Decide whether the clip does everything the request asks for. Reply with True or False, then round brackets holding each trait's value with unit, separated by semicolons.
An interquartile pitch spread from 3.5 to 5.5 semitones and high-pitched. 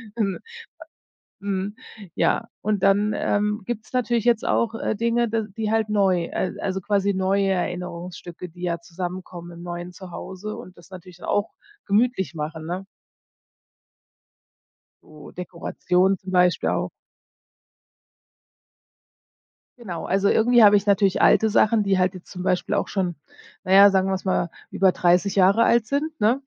False (2.8 semitones; 195 Hz)